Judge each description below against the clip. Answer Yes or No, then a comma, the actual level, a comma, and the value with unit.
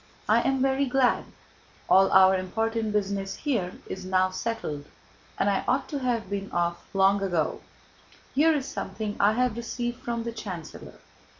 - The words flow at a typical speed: Yes, average, 160 wpm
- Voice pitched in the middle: No, high, 210 Hz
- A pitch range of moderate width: Yes, average, 4.2 semitones